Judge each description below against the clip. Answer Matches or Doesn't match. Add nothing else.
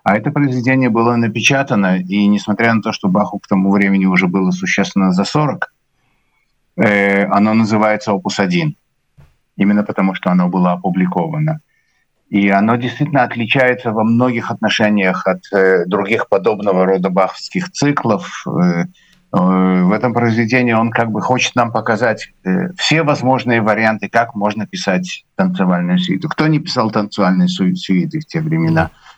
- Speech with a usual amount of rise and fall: Doesn't match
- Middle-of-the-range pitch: Doesn't match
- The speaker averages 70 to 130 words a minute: Doesn't match